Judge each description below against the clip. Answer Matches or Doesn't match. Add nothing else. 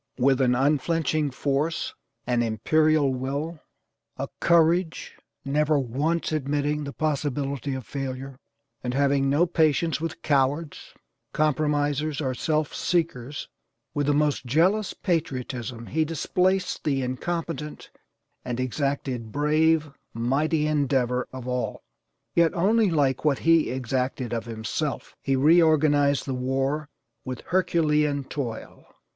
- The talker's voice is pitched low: Doesn't match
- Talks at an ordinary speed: Doesn't match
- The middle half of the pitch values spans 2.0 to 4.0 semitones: Matches